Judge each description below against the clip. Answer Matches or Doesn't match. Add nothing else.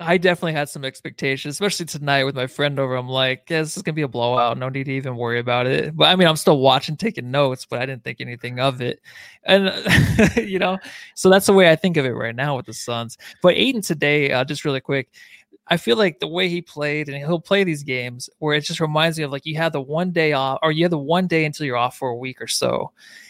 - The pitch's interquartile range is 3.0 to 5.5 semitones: Matches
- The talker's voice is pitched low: Doesn't match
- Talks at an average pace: Doesn't match